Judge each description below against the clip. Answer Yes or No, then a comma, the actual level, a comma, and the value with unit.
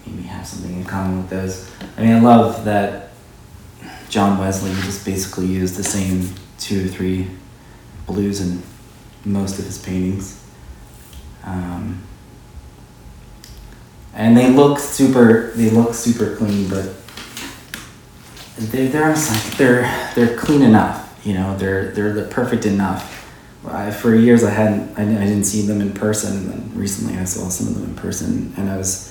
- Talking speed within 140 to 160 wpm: Yes, average, 150 wpm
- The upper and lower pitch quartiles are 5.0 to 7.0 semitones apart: No, average, 3.4 semitones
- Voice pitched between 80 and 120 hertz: Yes, low, 100 Hz